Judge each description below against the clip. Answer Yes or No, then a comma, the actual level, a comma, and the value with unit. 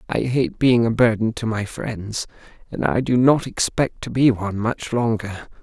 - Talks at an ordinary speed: Yes, average, 190 wpm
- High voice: No, low, 115 Hz